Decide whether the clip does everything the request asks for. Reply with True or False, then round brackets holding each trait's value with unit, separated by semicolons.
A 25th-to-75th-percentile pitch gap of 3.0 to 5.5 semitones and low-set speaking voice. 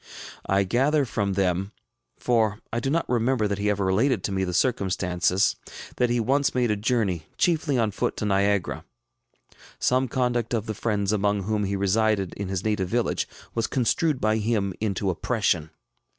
True (3.6 semitones; 105 Hz)